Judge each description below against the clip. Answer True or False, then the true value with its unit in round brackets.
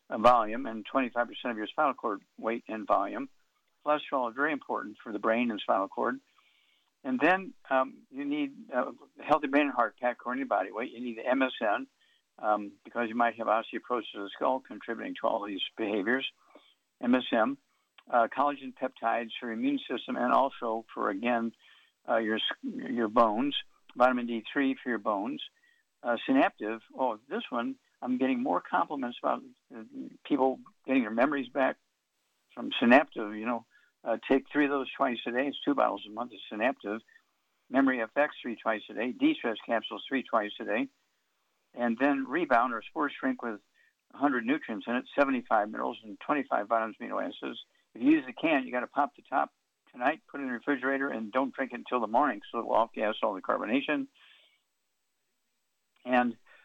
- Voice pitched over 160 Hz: False (135 Hz)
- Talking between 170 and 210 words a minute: True (180 wpm)